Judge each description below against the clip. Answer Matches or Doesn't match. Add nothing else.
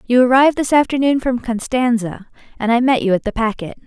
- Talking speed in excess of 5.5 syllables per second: Matches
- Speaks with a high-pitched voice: Matches